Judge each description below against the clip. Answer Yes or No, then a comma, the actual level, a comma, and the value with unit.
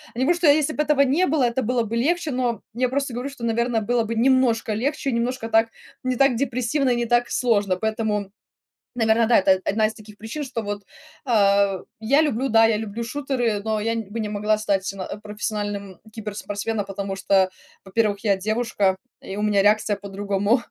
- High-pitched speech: Yes, high, 225 Hz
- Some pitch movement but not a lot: Yes, average, 3.4 semitones